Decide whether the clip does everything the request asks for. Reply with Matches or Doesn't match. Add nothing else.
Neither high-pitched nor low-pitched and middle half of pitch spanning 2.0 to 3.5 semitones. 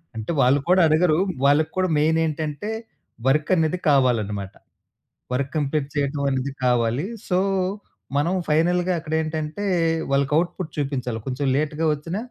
Matches